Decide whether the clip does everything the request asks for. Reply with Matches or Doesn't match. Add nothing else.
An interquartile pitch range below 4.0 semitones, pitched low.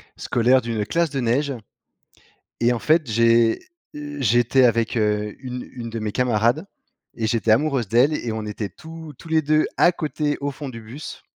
Doesn't match